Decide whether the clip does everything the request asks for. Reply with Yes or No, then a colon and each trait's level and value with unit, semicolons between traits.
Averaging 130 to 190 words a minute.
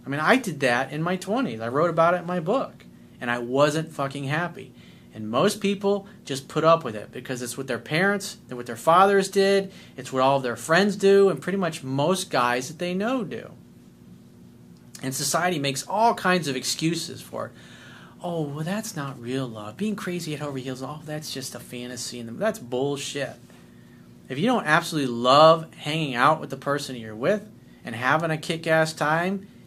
No: average, 200 wpm